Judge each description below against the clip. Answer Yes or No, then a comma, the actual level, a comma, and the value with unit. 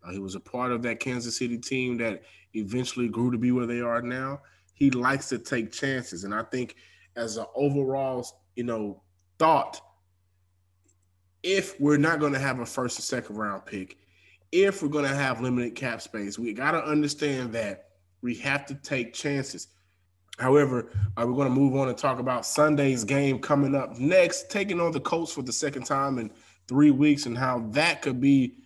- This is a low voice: Yes, low, 125 Hz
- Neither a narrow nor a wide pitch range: Yes, average, 4.0 semitones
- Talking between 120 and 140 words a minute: No, average, 195 wpm